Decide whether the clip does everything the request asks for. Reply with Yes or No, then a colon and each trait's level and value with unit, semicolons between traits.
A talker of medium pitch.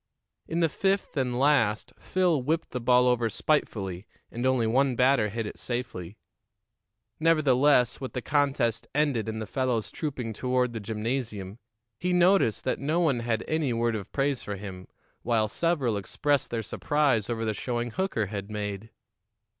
No: low, 125 Hz